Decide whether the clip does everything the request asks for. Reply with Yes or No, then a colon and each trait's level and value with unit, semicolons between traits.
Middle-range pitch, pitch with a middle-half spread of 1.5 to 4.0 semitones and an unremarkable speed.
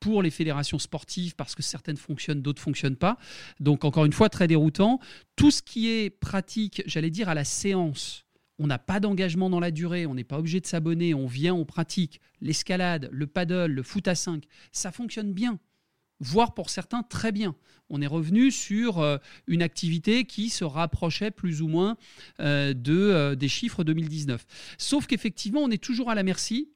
No: medium, 175 Hz; average, 5.2 semitones; average, 185 wpm